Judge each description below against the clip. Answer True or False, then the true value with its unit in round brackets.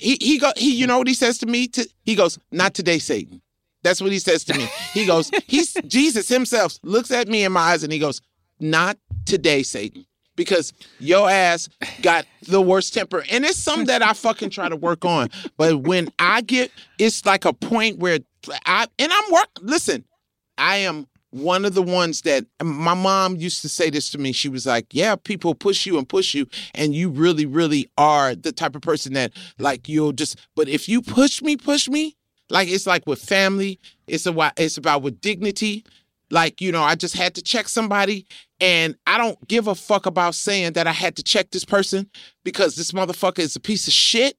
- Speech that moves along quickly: True (215 wpm)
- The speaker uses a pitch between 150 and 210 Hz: True (185 Hz)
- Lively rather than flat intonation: True (6.0 semitones)